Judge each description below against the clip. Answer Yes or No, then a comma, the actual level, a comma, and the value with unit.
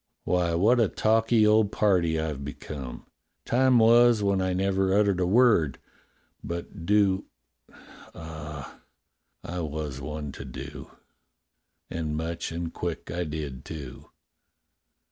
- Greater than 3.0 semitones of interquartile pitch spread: Yes, average, 5.1 semitones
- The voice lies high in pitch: No, very low, 85 Hz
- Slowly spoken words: Yes, slow, 130 wpm